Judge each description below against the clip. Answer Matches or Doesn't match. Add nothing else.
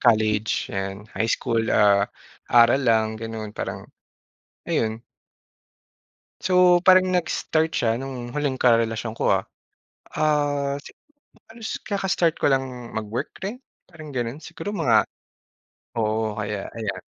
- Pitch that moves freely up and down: Matches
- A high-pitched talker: Doesn't match